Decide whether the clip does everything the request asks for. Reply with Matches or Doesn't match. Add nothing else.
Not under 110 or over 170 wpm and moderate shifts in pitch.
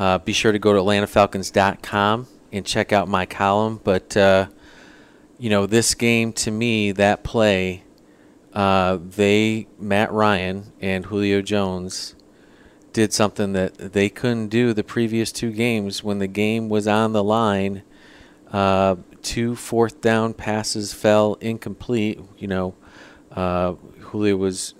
Doesn't match